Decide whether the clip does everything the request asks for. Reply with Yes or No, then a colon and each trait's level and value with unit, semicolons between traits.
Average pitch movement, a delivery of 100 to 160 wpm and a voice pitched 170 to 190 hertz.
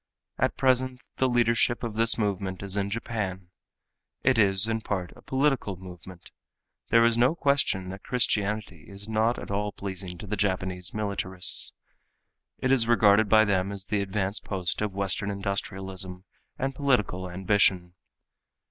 No: average, 3.4 semitones; average, 150 wpm; low, 100 Hz